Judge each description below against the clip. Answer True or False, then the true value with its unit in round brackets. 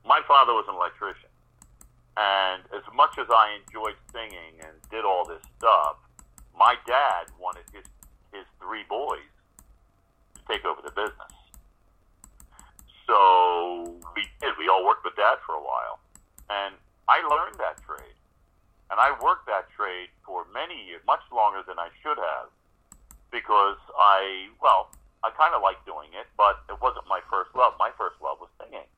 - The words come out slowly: False (165 wpm)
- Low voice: True (90 Hz)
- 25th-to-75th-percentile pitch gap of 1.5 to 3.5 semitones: True (2.8 semitones)